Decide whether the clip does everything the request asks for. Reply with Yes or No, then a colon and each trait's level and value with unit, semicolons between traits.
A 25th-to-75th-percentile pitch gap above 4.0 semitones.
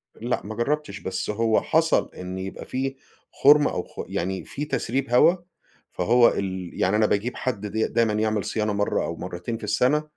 Yes: average, 4.4 semitones